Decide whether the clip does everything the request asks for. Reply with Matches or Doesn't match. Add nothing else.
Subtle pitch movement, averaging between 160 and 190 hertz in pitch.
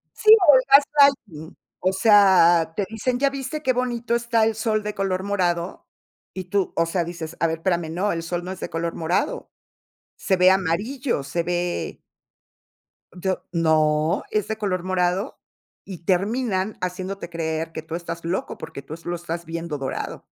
Doesn't match